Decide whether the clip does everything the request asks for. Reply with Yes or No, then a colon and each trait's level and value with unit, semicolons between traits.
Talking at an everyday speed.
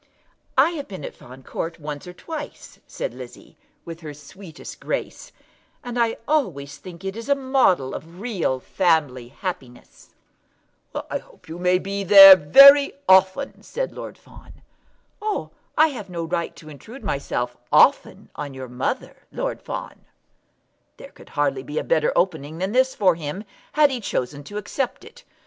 Yes: average, 160 wpm